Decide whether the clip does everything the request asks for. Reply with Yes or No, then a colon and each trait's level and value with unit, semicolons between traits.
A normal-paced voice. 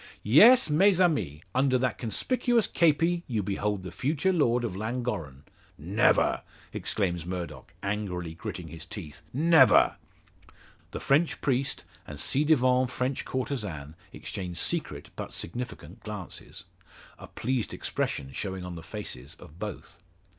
No: slow, 130 wpm